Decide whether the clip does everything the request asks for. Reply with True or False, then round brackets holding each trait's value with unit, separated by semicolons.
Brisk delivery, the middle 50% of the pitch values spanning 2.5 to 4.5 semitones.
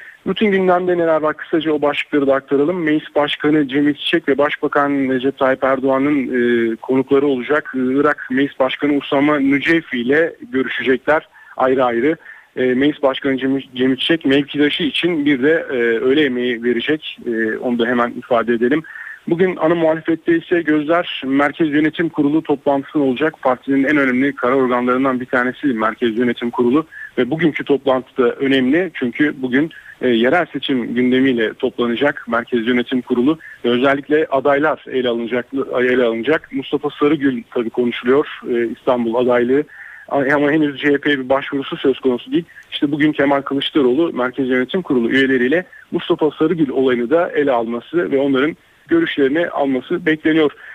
True (145 wpm; 3.2 semitones)